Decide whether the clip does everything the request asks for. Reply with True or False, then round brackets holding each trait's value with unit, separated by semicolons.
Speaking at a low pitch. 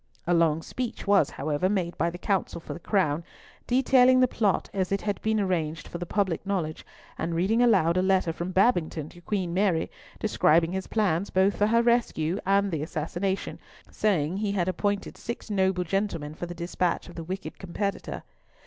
False (185 Hz)